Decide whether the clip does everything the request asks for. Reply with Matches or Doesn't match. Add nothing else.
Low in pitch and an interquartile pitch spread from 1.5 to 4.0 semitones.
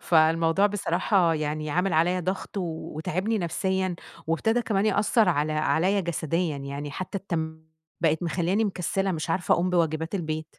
Doesn't match